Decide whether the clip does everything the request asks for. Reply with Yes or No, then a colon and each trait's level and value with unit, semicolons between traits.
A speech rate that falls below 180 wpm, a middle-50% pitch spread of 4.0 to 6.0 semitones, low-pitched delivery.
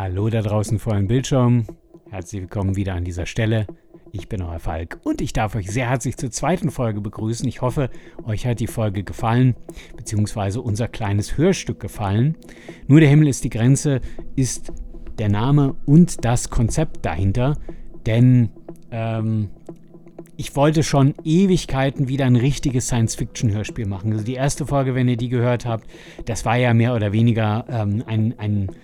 Yes: average, 165 wpm; average, 4.6 semitones; low, 120 Hz